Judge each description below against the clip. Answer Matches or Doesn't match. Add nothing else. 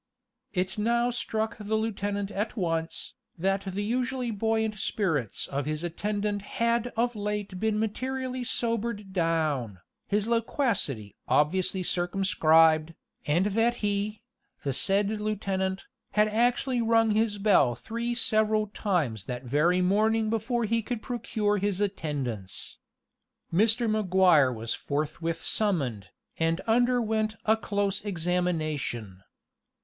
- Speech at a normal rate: Doesn't match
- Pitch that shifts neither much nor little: Matches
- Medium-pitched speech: Doesn't match